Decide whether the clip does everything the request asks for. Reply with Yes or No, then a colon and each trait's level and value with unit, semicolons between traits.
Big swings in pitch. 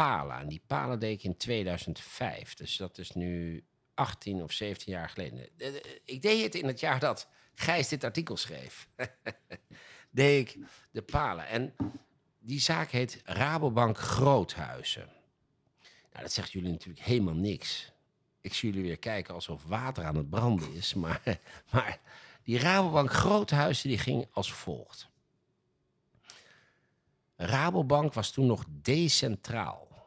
Yes: wide, 7.0 semitones